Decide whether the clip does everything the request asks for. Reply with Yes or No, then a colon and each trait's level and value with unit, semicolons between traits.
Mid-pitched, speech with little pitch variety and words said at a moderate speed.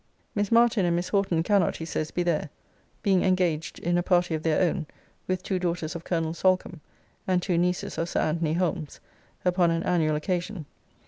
Yes: medium, 175 Hz; narrow, 2.1 semitones; average, 190 wpm